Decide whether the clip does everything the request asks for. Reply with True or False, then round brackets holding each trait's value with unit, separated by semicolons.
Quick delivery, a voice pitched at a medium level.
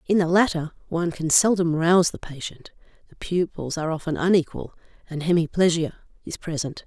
False (155 wpm; 165 Hz)